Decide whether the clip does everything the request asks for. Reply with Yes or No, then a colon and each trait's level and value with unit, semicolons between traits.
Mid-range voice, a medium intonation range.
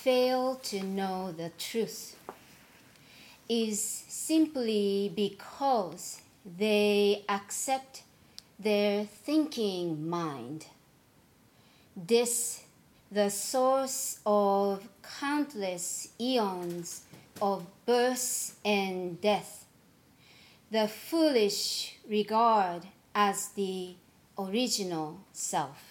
No: high, 205 Hz; average, 3.4 semitones